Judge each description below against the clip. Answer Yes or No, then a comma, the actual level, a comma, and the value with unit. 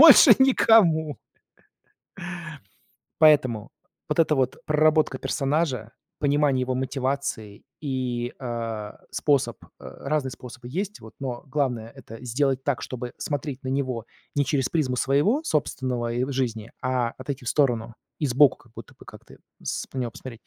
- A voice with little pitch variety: No, average, 3.3 semitones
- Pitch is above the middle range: No, low, 130 Hz